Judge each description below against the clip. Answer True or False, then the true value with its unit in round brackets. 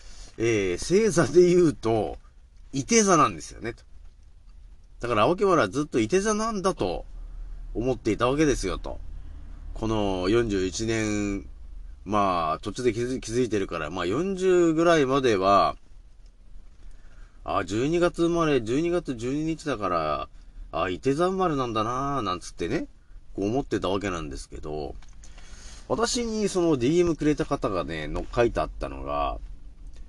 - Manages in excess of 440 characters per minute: False (265 characters per minute)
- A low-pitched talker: True (110 Hz)